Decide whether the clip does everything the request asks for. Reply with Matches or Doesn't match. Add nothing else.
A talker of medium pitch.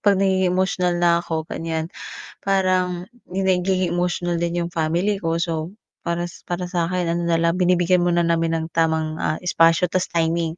Matches